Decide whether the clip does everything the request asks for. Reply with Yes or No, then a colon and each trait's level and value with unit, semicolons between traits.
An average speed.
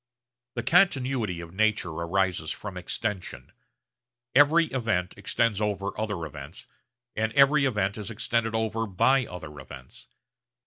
No: slow, 125 wpm